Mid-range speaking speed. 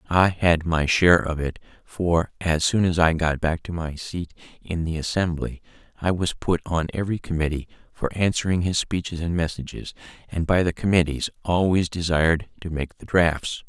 Yes: average, 180 wpm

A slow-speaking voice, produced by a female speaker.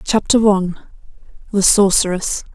Yes: slow, 95 wpm; female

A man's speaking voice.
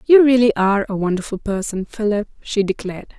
No: female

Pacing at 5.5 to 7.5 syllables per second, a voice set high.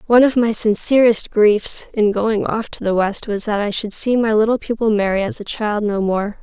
No: 5.0 syllables/s; high, 215 Hz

